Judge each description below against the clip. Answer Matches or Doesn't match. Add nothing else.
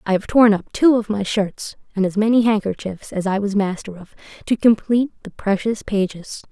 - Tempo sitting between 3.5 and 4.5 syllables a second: Doesn't match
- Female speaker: Matches